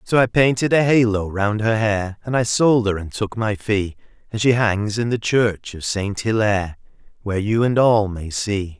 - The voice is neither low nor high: No, low, 110 Hz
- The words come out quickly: Yes, fast, 210 wpm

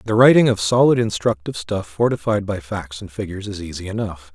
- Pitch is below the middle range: Yes, low, 100 Hz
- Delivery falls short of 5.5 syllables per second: No, 5.9 syllables/s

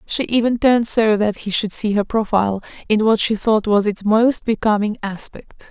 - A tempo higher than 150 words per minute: Yes, average, 200 wpm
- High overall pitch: Yes, high, 215 Hz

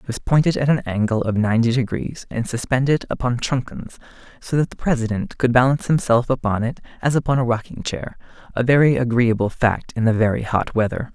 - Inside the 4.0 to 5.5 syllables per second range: No, 5.8 syllables/s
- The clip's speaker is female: No, male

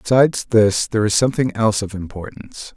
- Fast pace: No, average, 195 wpm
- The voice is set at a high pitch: No, low, 110 Hz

